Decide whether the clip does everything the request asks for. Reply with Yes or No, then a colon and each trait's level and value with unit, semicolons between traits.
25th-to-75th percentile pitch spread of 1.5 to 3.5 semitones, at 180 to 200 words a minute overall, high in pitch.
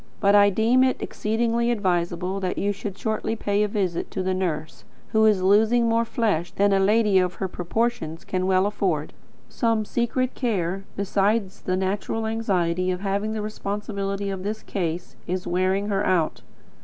No: average, 2.8 semitones; average, 170 wpm; high, 200 Hz